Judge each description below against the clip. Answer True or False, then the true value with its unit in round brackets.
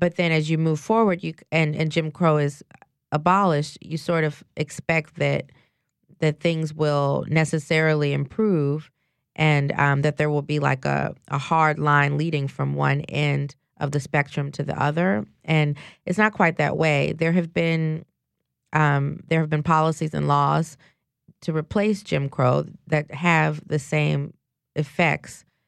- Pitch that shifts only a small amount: True (2.2 semitones)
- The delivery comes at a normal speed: True (160 wpm)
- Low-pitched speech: False (155 Hz)